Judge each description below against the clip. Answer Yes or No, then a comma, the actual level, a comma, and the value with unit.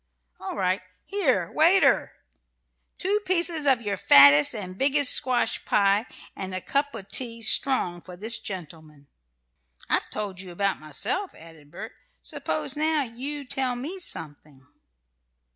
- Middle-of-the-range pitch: No, high, 215 Hz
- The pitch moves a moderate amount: No, wide, 8.2 semitones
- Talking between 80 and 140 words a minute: Yes, slow, 135 wpm